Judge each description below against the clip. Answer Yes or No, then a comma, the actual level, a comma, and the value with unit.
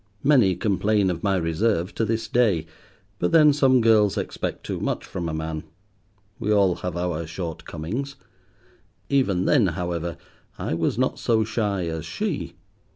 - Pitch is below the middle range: Yes, very low, 95 Hz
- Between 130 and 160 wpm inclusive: Yes, average, 155 wpm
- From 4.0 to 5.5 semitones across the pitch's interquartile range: Yes, average, 5.2 semitones